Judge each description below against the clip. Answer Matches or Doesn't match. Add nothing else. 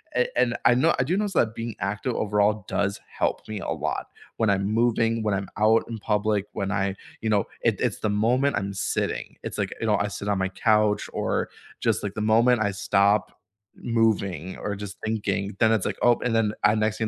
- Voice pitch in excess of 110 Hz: Doesn't match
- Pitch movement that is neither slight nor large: Doesn't match